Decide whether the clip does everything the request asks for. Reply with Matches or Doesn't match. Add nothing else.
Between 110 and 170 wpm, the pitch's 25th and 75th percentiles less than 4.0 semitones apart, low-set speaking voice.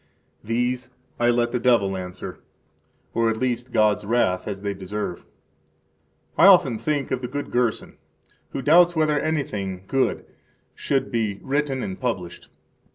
Doesn't match